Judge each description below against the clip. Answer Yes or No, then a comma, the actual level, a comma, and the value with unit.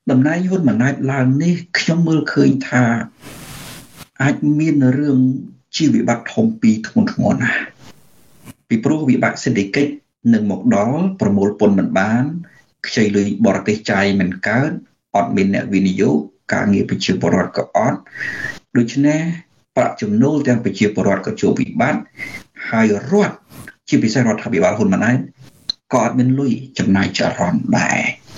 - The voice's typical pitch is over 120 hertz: Yes, low, 135 Hz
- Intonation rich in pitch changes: Yes, wide, 6.7 semitones